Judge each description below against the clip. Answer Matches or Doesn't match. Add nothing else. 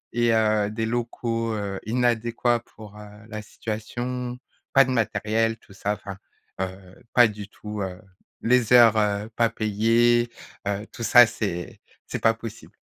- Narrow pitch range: Matches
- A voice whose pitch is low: Matches